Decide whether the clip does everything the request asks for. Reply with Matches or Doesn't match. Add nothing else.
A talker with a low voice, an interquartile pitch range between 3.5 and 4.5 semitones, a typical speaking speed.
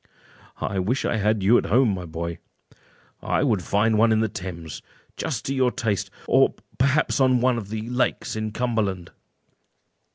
Matches